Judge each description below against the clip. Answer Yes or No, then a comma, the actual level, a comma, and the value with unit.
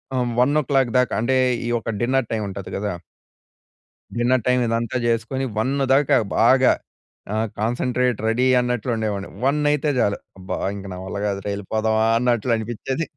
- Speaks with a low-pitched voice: Yes, low, 120 Hz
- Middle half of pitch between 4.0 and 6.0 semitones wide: No, average, 2.9 semitones